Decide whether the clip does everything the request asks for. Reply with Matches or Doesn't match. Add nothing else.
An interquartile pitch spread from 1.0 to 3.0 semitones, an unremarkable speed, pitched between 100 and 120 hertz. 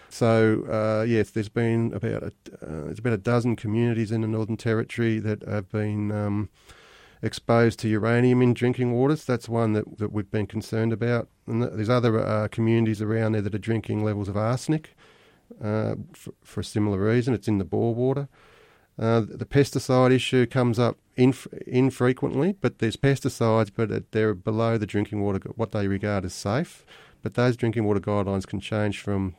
Matches